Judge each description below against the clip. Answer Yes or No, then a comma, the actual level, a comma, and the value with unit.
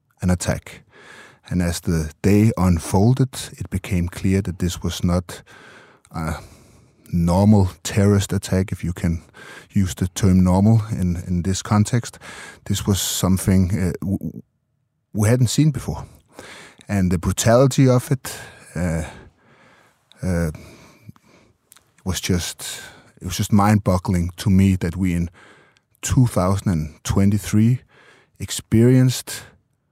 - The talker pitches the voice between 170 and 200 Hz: No, very low, 95 Hz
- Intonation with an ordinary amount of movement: Yes, average, 3.2 semitones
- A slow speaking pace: Yes, slow, 115 wpm